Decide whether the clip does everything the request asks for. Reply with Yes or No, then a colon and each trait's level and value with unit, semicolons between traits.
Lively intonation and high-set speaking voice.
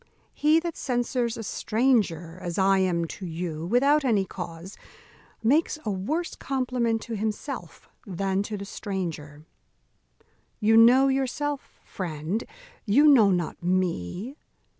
Yes: wide, 6.0 semitones; high, 210 Hz